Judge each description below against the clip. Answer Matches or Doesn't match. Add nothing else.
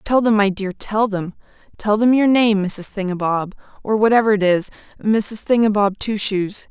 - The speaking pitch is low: Doesn't match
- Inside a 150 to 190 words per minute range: Matches